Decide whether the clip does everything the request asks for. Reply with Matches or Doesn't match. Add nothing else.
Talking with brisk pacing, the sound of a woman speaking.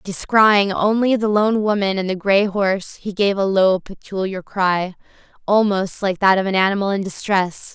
Doesn't match